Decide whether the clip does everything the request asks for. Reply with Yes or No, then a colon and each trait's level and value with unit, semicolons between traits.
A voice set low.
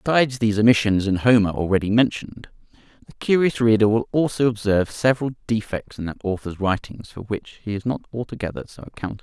Yes: low, 110 Hz